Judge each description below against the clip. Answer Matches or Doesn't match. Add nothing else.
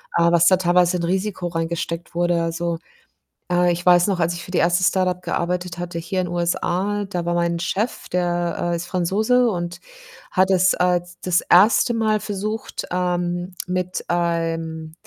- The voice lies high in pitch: Doesn't match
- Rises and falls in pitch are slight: Matches